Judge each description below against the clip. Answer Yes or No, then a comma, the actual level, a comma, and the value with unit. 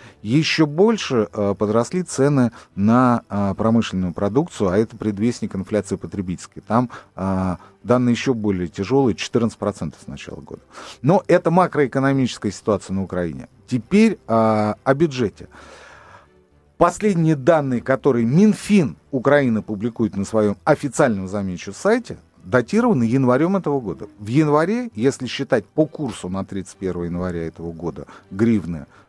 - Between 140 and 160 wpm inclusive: No, average, 120 wpm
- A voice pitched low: Yes, low, 115 Hz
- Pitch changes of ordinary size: No, wide, 6.3 semitones